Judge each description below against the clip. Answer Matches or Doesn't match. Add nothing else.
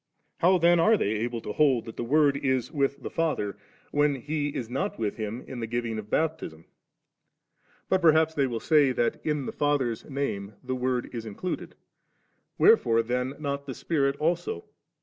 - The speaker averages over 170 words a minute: Matches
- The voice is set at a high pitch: Doesn't match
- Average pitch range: Matches